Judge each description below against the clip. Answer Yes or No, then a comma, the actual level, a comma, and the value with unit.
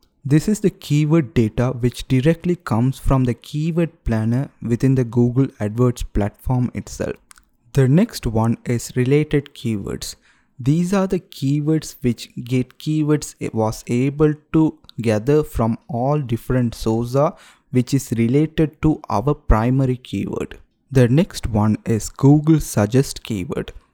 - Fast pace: No, slow, 135 wpm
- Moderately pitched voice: No, low, 130 Hz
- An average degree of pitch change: Yes, average, 4.4 semitones